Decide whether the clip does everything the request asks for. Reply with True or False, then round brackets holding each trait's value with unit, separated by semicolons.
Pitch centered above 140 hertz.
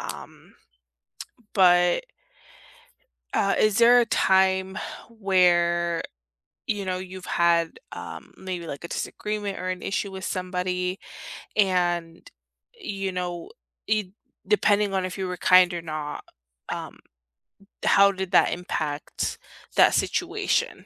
True (185 Hz)